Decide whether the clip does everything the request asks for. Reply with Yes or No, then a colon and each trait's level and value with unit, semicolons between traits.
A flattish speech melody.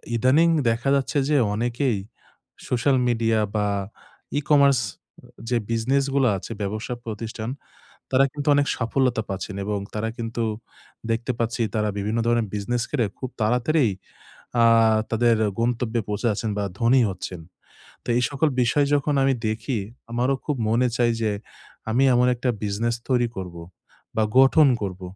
No: average, 3.1 semitones